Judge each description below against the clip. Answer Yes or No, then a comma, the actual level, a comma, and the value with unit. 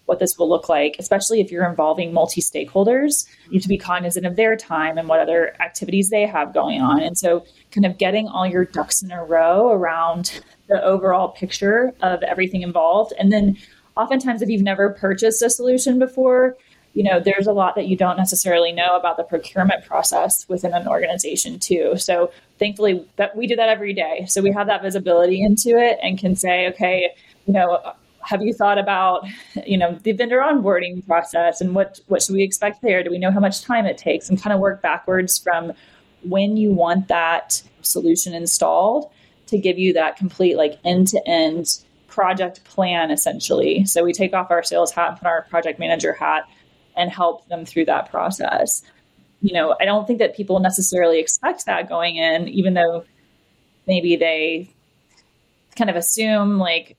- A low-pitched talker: No, medium, 185 Hz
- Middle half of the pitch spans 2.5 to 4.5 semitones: Yes, average, 3.3 semitones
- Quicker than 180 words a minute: Yes, average, 190 wpm